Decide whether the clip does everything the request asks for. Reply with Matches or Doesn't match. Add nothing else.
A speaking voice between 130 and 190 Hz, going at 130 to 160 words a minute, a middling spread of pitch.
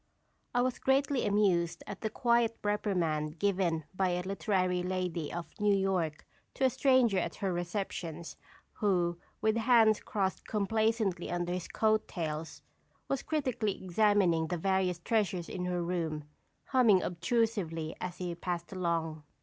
Matches